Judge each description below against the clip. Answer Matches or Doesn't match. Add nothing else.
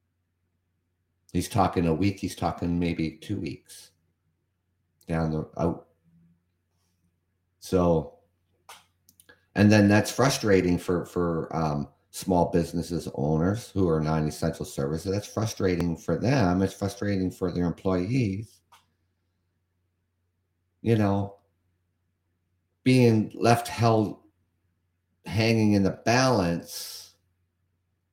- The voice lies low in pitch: Matches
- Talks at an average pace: Doesn't match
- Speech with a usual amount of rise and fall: Doesn't match